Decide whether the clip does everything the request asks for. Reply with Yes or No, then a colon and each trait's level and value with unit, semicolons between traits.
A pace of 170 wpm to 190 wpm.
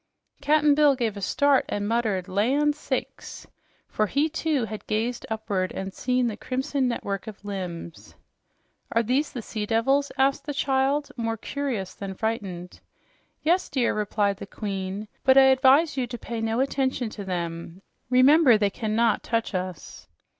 No: average, 160 wpm